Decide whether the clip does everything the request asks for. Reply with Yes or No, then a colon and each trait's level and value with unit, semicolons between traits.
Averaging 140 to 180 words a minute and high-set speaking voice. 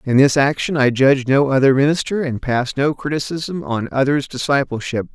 No: average, 175 wpm; medium, 140 Hz